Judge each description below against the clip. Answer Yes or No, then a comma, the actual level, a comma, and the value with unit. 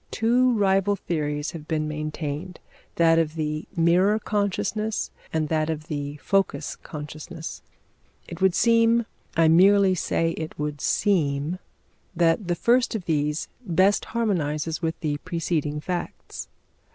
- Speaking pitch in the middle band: Yes, medium, 165 Hz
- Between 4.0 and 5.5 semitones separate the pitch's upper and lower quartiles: Yes, average, 4.3 semitones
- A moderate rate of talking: No, slow, 130 wpm